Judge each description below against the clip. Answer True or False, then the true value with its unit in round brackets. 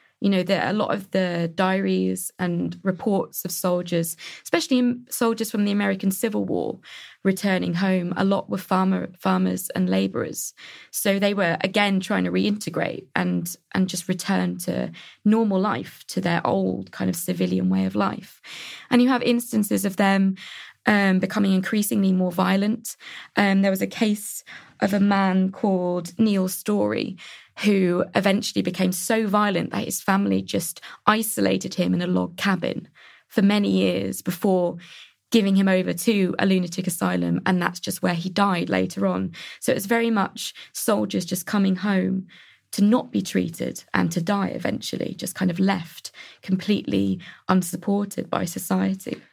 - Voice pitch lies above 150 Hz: True (190 Hz)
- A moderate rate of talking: True (160 wpm)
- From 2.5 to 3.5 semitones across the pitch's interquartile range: True (3.1 semitones)